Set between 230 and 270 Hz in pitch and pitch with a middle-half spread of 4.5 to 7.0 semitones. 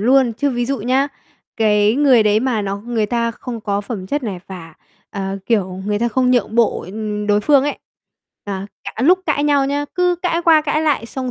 Yes: high, 235 Hz; average, 4.9 semitones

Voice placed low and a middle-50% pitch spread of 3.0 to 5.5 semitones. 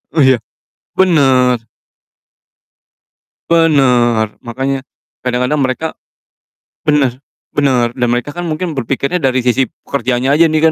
Yes: low, 130 Hz; average, 3.5 semitones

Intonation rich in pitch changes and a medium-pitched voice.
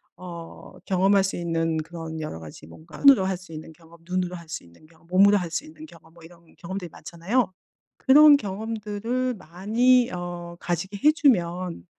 No: average, 4.0 semitones; medium, 180 Hz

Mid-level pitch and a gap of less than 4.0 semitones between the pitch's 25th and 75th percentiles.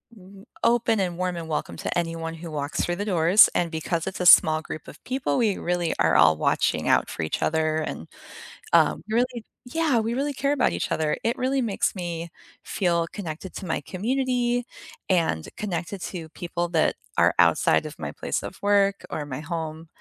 No: medium, 175 Hz; average, 5.3 semitones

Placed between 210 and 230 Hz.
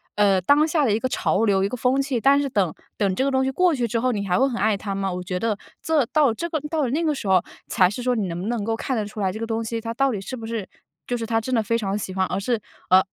Yes: high, 225 Hz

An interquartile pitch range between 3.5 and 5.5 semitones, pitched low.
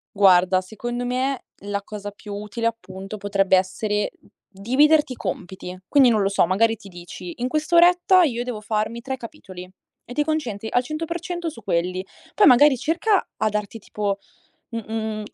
No: average, 5.0 semitones; high, 220 Hz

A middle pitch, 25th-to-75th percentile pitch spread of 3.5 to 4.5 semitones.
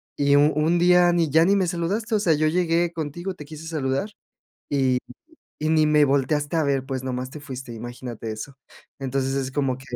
Yes: medium, 145 Hz; average, 4.0 semitones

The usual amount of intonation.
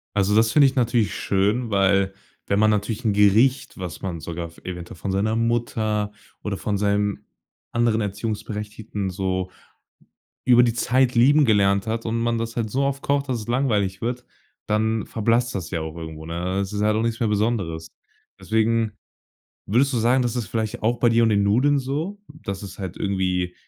Yes: average, 3.2 semitones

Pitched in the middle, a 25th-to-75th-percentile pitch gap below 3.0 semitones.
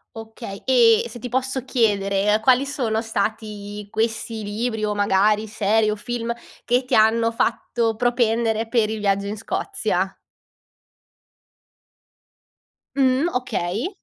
No: high, 220 Hz; narrow, 2.4 semitones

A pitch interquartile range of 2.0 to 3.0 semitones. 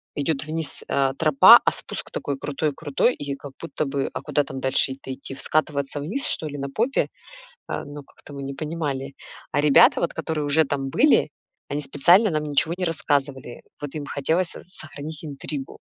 Yes: narrow, 2.5 semitones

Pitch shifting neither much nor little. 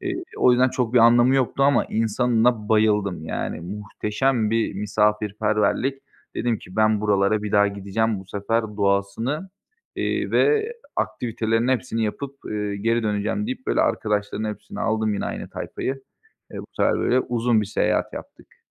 Yes: average, 3.0 semitones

